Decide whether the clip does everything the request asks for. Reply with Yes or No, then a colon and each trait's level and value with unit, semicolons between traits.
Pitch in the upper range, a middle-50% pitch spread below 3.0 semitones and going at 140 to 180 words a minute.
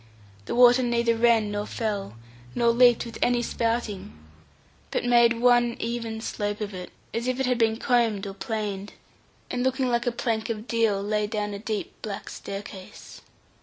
Yes: high, 230 Hz; narrow, 2.5 semitones; average, 170 wpm